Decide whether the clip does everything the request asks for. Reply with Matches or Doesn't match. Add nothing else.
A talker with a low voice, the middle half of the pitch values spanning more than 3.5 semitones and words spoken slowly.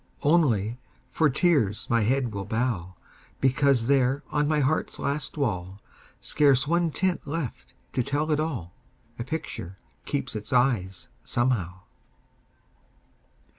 Matches